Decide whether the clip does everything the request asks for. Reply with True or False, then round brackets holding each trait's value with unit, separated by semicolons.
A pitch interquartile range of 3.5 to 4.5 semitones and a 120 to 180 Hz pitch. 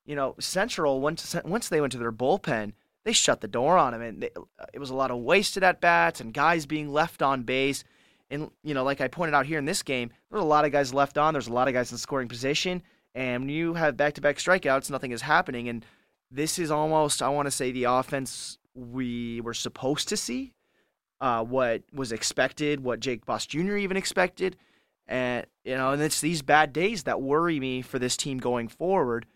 True (3.9 semitones; 140 Hz)